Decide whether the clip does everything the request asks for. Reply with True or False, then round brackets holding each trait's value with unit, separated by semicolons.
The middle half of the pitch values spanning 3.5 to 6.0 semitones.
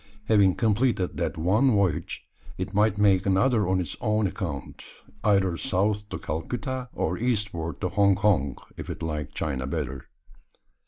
True (4.2 semitones)